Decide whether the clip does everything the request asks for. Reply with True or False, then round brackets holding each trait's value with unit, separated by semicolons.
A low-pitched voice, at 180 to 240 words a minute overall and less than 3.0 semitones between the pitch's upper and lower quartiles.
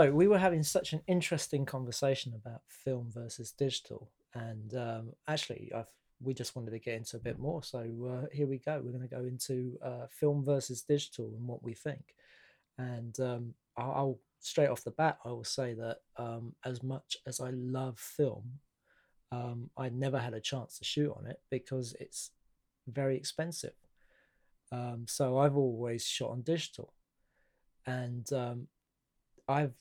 False (130 Hz; 170 wpm; 2.6 semitones)